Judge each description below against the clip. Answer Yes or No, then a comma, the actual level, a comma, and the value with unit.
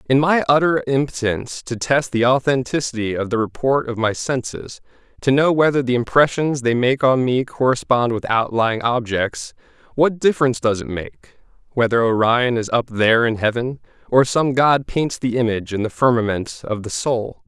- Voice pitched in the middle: No, low, 125 Hz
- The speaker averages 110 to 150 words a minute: No, average, 175 wpm